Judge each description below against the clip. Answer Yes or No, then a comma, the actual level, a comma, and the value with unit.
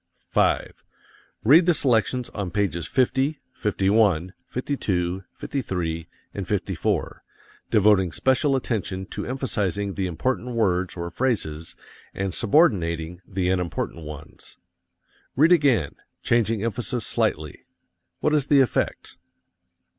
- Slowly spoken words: Yes, slow, 110 wpm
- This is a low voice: Yes, low, 105 Hz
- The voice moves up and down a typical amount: No, wide, 6.3 semitones